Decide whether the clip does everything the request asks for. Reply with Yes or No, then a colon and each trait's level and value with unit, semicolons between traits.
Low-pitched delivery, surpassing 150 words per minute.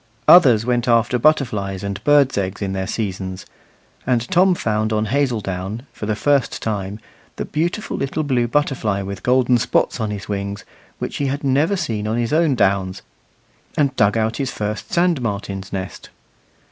Yes: low, 115 Hz; average, 170 wpm